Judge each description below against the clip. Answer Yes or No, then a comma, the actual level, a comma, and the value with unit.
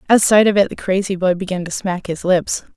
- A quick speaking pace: Yes, fast, 260 wpm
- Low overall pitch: No, high, 190 Hz